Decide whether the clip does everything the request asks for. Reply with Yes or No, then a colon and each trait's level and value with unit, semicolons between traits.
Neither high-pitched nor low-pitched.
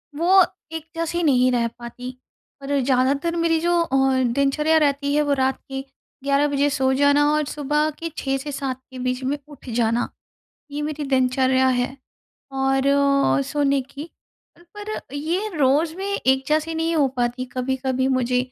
No: very high, 275 Hz